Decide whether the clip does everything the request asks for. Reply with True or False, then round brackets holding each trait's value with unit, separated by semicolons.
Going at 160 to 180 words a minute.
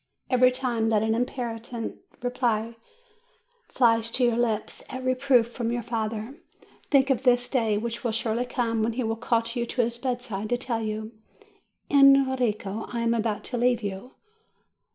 True (170 wpm)